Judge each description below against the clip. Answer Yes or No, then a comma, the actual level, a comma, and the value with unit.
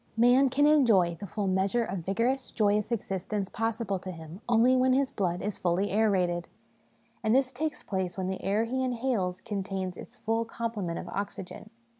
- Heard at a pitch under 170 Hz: No, high, 210 Hz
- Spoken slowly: No, average, 175 wpm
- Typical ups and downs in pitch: Yes, average, 4.2 semitones